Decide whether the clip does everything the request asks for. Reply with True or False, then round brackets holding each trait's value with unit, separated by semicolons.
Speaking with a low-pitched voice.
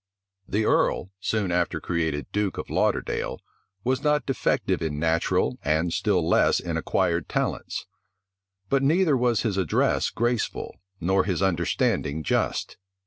True (95 Hz)